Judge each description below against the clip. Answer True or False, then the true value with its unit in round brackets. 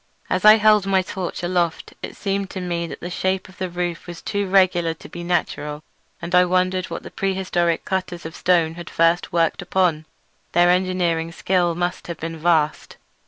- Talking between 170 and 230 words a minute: True (190 wpm)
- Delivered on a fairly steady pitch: True (1.8 semitones)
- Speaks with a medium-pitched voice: True (175 Hz)